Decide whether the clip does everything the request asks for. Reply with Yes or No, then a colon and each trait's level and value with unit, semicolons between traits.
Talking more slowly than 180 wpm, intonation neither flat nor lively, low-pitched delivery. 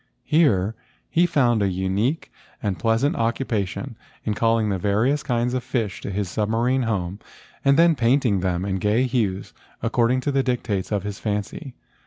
Yes: average, 170 wpm; average, 4.3 semitones; low, 115 Hz